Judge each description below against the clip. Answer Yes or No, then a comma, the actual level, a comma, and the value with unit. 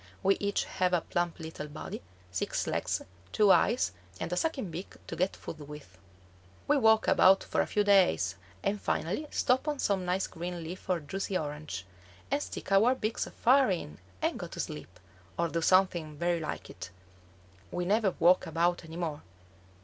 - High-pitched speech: No, medium, 180 Hz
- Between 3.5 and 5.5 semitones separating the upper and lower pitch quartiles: Yes, average, 4.0 semitones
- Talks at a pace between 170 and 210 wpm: Yes, average, 180 wpm